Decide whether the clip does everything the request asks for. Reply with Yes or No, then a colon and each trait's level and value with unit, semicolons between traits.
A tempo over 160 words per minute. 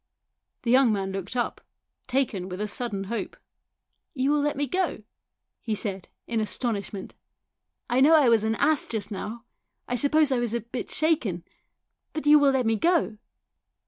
Yes: average, 185 wpm